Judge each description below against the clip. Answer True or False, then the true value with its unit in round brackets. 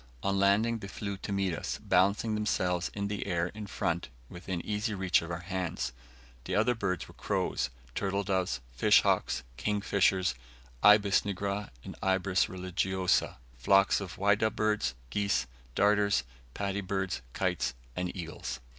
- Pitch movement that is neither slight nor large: False (2.0 semitones)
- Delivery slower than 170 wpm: True (145 wpm)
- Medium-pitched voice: False (95 Hz)